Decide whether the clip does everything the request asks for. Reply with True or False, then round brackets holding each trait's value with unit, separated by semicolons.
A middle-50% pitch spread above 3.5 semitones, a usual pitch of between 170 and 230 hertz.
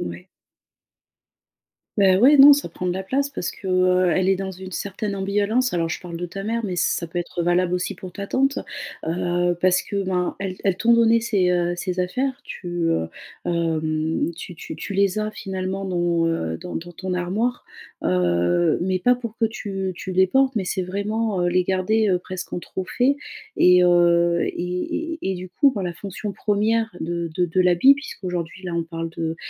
False (2.8 semitones; 185 Hz)